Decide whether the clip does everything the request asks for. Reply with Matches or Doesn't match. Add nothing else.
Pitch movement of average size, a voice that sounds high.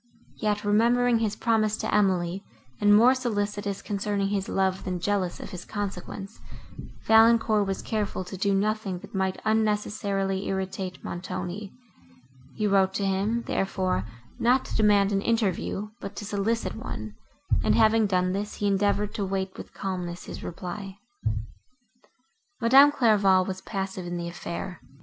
Doesn't match